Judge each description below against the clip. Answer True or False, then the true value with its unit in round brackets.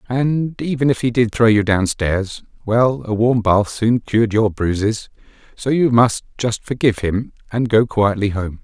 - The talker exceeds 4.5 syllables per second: False (4.4 syllables/s)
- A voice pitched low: True (115 Hz)